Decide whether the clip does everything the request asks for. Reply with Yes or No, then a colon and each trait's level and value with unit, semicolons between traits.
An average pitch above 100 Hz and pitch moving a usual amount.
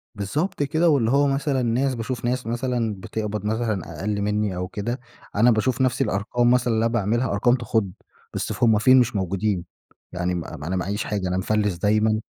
Yes: low, 110 Hz; average, 3.5 semitones